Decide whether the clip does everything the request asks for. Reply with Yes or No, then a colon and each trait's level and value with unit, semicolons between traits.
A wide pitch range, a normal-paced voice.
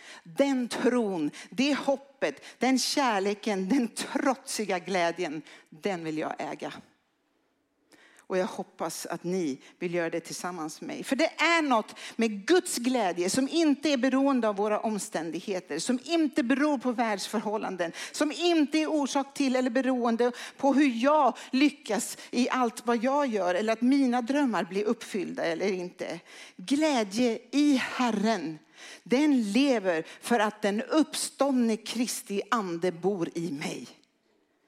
Yes: wide, 5.8 semitones; average, 140 wpm